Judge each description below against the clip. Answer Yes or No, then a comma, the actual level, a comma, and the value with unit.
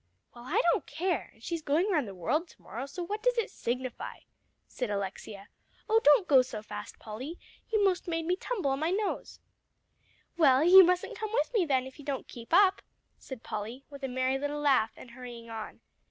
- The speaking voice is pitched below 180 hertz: No, very high, 280 Hz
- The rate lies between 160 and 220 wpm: Yes, fast, 205 wpm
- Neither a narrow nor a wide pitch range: No, wide, 6.7 semitones